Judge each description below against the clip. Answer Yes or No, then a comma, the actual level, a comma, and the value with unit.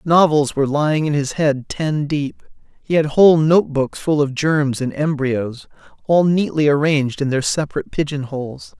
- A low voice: No, medium, 145 Hz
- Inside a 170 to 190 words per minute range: Yes, average, 175 wpm